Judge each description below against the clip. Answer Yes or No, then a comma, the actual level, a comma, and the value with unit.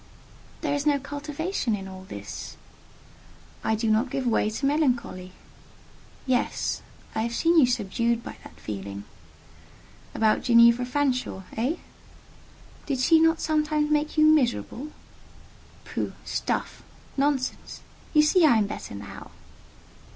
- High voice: Yes, very high, 255 Hz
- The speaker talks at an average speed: No, slow, 125 wpm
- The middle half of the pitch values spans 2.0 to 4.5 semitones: No, average, 5.3 semitones